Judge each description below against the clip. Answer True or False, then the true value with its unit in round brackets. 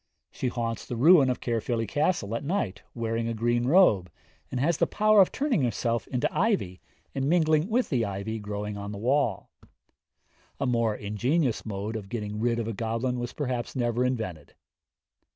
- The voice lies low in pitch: True (120 Hz)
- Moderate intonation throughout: True (4.4 semitones)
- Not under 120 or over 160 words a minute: False (175 wpm)